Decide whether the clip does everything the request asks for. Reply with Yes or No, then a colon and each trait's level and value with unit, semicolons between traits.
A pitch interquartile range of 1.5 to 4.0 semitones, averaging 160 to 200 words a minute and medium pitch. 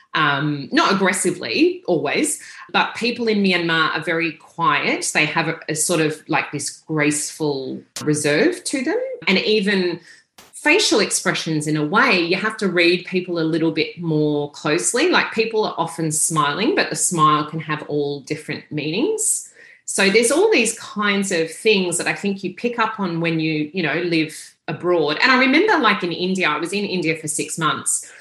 No: average, 4.7 semitones; average, 185 wpm; medium, 170 Hz